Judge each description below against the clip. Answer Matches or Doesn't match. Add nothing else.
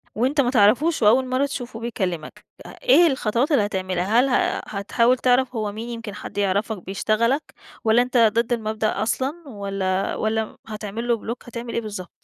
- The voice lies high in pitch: Matches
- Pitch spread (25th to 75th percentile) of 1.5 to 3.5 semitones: Matches